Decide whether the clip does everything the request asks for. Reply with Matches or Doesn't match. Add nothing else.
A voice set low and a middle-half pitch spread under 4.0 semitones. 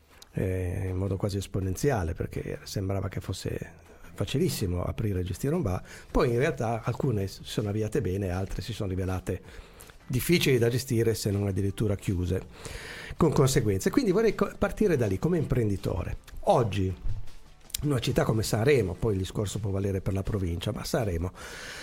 Doesn't match